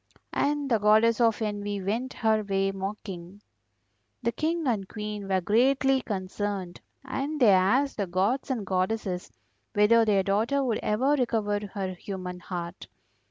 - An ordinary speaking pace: Yes, average, 145 wpm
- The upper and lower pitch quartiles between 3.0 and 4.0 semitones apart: Yes, average, 3.6 semitones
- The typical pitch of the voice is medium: No, high, 210 Hz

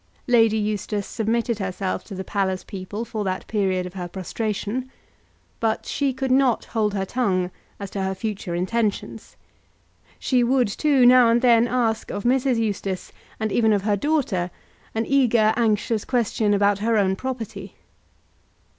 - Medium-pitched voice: No, high, 220 Hz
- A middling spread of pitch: Yes, average, 3.4 semitones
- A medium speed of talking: Yes, average, 155 wpm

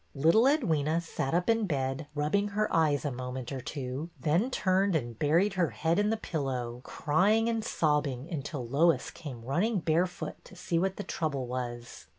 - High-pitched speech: No, medium, 155 Hz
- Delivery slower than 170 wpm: No, average, 175 wpm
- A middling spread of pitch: No, wide, 5.8 semitones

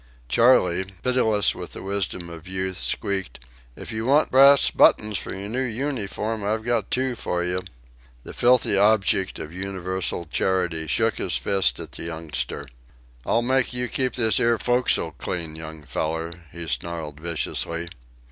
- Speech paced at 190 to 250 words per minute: No, average, 155 wpm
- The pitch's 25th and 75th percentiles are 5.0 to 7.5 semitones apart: Yes, wide, 5.5 semitones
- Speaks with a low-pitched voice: Yes, very low, 95 Hz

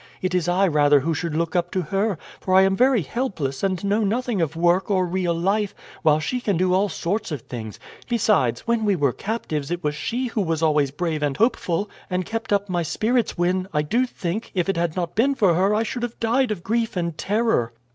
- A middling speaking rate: No, fast, 230 wpm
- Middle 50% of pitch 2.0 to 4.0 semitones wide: No, average, 4.7 semitones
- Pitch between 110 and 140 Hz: No, medium, 185 Hz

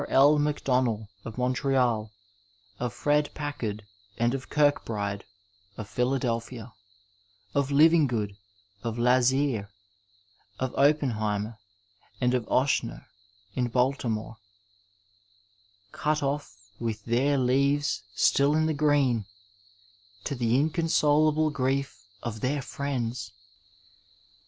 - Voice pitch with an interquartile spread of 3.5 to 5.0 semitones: Yes, average, 4.1 semitones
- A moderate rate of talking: No, slow, 105 wpm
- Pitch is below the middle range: Yes, low, 125 Hz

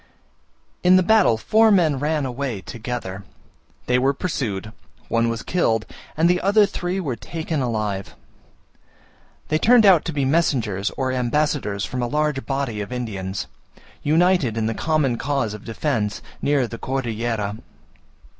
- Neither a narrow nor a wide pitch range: No, wide, 5.8 semitones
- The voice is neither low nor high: No, low, 130 Hz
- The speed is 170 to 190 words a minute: No, average, 145 wpm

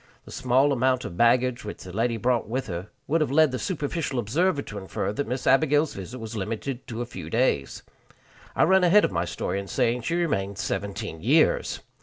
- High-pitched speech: No, low, 120 Hz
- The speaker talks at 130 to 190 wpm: No, fast, 205 wpm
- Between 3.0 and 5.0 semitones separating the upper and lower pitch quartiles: No, wide, 5.5 semitones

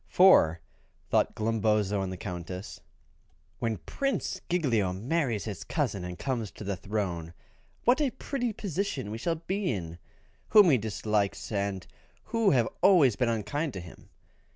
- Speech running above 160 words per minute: No, average, 150 wpm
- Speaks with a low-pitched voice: Yes, low, 110 Hz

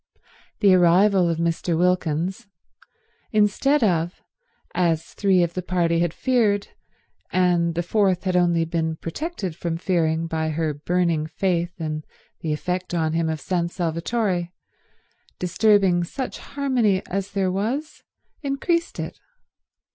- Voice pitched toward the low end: No, medium, 180 Hz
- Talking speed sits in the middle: No, slow, 130 wpm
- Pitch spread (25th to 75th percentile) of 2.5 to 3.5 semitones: Yes, average, 3.2 semitones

